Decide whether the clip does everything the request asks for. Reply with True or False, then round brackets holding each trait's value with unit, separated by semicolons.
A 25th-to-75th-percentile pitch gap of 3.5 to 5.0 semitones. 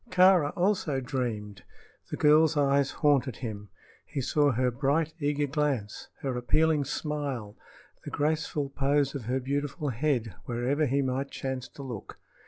False (2.9 semitones)